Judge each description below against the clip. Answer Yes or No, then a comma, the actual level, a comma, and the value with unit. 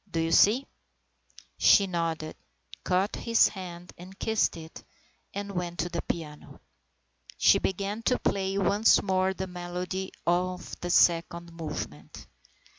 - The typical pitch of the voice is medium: Yes, medium, 180 Hz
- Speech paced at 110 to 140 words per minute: Yes, slow, 135 wpm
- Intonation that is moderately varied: No, narrow, 2.3 semitones